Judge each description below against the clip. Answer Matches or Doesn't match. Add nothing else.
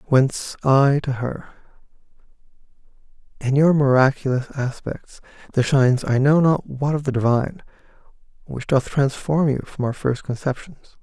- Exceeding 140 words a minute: Doesn't match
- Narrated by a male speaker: Matches